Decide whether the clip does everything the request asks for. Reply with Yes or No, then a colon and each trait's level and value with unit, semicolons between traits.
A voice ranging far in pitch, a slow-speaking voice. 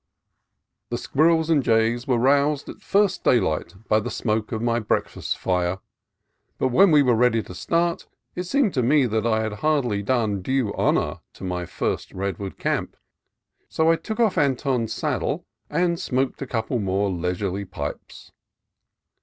No: wide, 6.5 semitones; average, 165 wpm